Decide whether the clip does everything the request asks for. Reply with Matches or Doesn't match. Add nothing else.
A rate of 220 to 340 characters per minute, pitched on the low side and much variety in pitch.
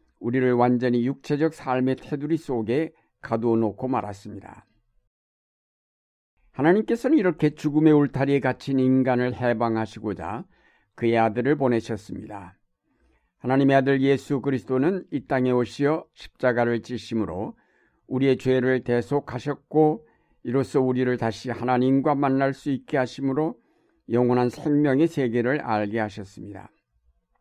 Doesn't match